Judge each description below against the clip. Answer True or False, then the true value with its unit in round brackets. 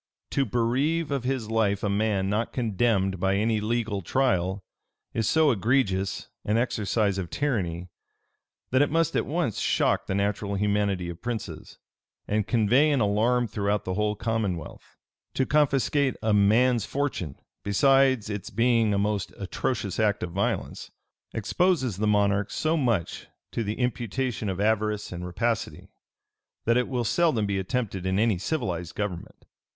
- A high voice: False (110 Hz)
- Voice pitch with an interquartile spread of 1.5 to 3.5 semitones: False (3.9 semitones)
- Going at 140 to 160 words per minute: True (150 wpm)